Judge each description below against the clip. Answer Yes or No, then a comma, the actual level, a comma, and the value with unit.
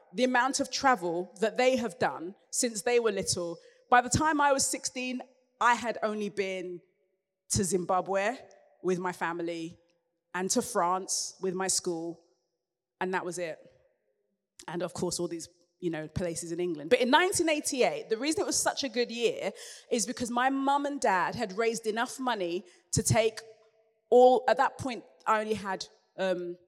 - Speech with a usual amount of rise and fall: No, wide, 5.9 semitones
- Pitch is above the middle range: Yes, high, 210 Hz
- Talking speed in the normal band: Yes, average, 175 wpm